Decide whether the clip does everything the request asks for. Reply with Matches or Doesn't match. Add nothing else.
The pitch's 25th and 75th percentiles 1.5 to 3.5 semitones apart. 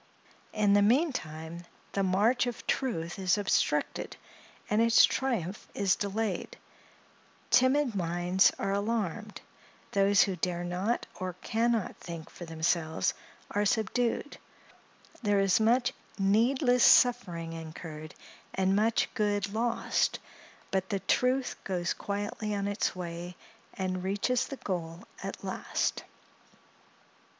Doesn't match